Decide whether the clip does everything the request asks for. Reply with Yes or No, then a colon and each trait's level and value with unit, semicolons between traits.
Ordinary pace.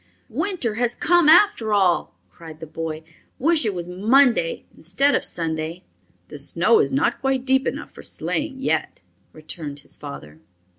Yes: average, 155 wpm